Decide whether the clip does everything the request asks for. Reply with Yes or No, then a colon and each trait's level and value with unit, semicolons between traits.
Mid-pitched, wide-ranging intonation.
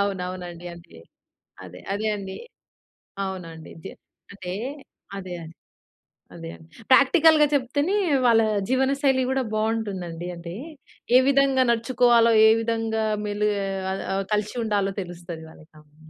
No: high, 205 Hz; wide, 5.8 semitones